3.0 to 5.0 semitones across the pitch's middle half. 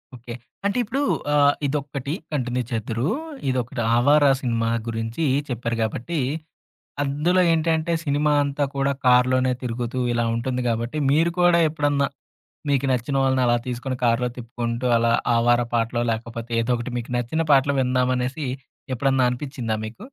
Yes: average, 3.3 semitones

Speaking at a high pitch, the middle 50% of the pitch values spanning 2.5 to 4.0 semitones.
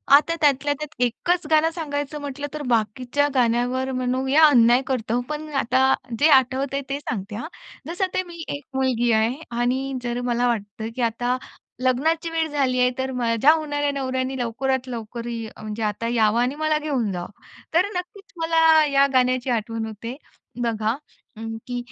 Yes: very high, 260 Hz; average, 3.5 semitones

